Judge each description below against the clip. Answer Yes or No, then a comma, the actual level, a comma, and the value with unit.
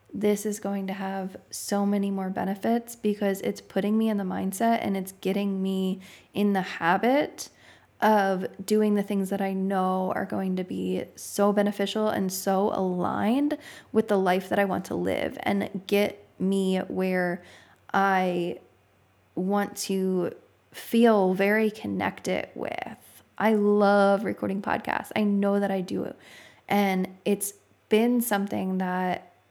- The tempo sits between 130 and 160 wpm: Yes, average, 145 wpm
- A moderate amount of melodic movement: No, narrow, 1.6 semitones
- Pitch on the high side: Yes, high, 195 Hz